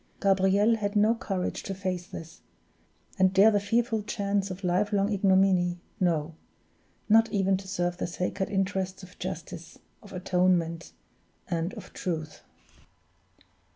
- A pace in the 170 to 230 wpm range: No, slow, 135 wpm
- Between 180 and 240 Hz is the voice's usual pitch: Yes, high, 190 Hz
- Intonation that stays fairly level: Yes, narrow, 2.2 semitones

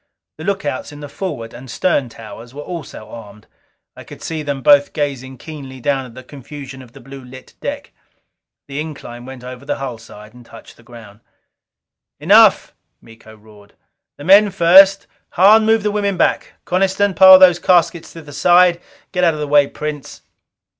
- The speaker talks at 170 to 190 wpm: Yes, average, 180 wpm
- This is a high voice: No, medium, 145 Hz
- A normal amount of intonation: No, wide, 6.0 semitones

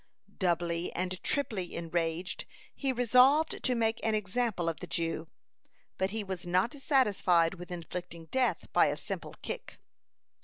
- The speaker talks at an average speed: Yes, average, 150 wpm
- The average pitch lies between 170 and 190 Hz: Yes, medium, 185 Hz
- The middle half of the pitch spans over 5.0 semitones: Yes, wide, 5.6 semitones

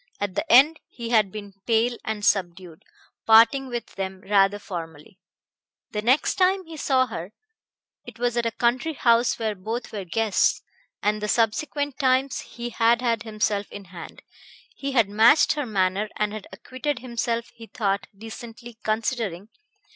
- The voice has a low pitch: No, high, 225 Hz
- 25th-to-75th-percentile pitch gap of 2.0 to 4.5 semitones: Yes, average, 3.2 semitones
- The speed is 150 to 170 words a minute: Yes, average, 160 wpm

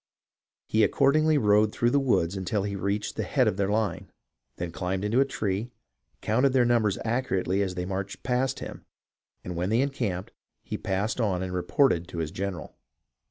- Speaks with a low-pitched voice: Yes, low, 100 Hz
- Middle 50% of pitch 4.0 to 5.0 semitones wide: Yes, average, 4.4 semitones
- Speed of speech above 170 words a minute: Yes, average, 185 wpm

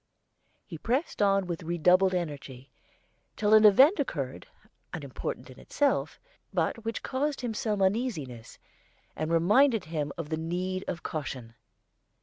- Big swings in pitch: Yes, wide, 5.8 semitones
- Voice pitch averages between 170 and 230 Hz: Yes, medium, 185 Hz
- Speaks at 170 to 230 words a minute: No, slow, 135 wpm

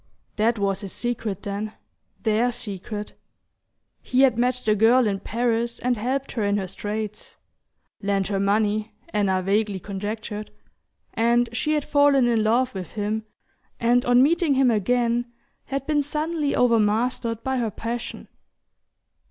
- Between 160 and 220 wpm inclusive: No, average, 145 wpm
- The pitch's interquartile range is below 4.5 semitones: Yes, average, 3.0 semitones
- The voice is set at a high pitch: Yes, high, 230 Hz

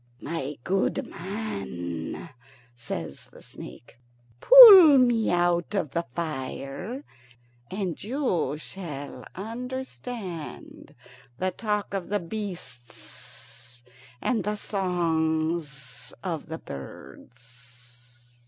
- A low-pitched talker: No, medium, 170 Hz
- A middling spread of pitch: No, wide, 8.1 semitones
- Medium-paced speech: No, slow, 90 wpm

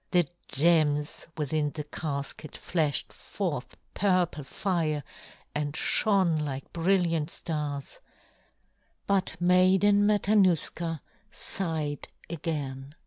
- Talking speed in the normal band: No, slow, 85 wpm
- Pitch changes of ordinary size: Yes, average, 3.6 semitones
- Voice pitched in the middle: Yes, medium, 160 Hz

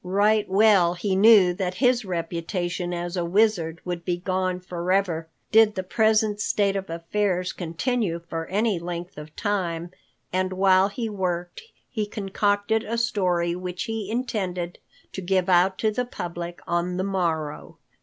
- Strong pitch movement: No, average, 2.9 semitones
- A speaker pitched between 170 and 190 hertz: Yes, medium, 185 Hz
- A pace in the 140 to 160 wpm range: Yes, average, 155 wpm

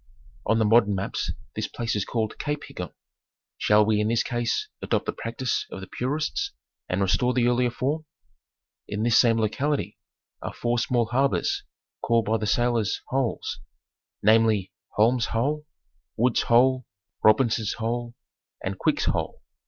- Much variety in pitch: No, average, 2.7 semitones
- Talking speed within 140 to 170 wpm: Yes, average, 150 wpm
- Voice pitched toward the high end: No, low, 115 Hz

